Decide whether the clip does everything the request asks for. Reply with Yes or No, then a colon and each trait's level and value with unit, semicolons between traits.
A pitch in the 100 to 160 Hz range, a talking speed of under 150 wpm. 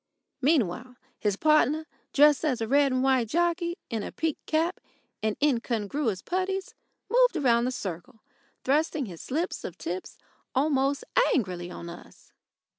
No: very high, 265 Hz; average, 140 wpm